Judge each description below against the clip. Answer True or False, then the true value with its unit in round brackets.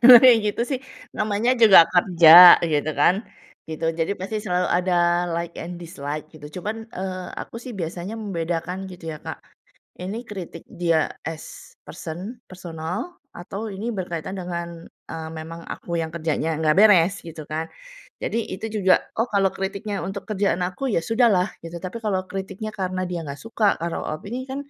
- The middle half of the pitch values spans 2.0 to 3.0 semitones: False (3.5 semitones)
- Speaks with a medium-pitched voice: True (180 Hz)